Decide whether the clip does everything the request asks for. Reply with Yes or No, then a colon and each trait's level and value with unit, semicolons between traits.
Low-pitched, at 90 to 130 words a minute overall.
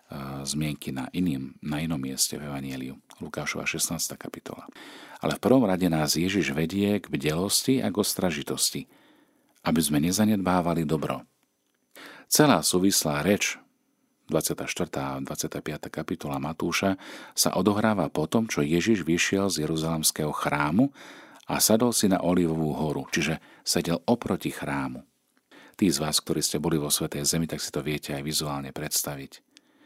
No: very low, 80 Hz; average, 145 wpm